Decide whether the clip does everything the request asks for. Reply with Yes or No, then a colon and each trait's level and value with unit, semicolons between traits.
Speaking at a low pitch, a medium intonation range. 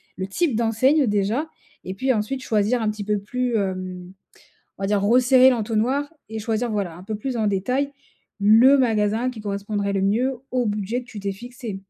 No: high, 220 Hz; average, 3.7 semitones